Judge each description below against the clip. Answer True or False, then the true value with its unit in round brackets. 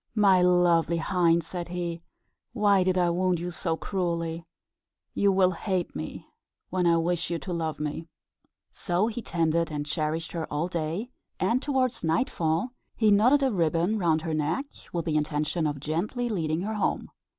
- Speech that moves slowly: False (170 wpm)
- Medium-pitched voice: True (175 Hz)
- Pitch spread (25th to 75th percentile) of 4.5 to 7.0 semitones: False (3.0 semitones)